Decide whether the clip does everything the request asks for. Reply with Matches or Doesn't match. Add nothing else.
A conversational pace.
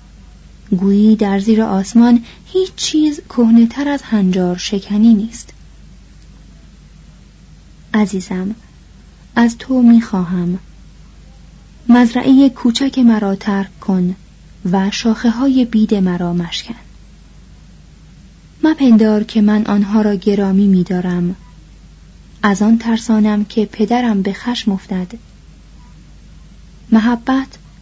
Doesn't match